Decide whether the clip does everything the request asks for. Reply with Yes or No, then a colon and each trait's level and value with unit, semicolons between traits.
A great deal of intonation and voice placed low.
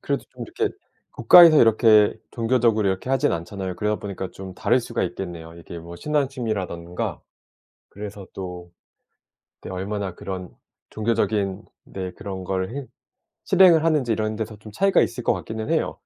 No: average, 4.0 semitones; low, 105 Hz